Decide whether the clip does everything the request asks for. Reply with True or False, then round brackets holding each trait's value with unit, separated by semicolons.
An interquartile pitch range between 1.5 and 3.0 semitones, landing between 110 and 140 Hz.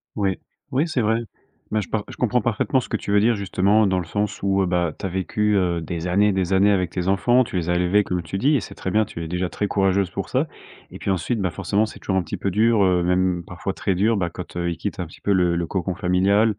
False (2.7 semitones; 95 Hz)